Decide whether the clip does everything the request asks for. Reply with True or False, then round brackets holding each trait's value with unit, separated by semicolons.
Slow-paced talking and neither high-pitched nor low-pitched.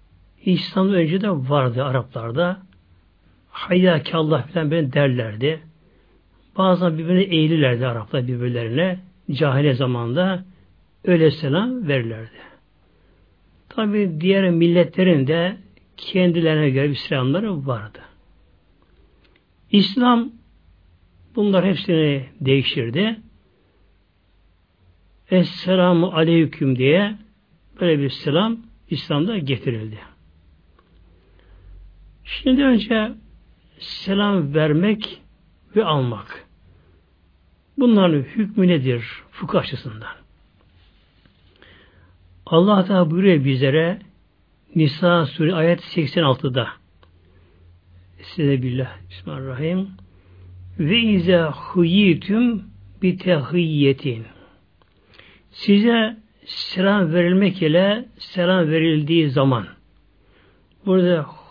True (75 wpm; 145 Hz)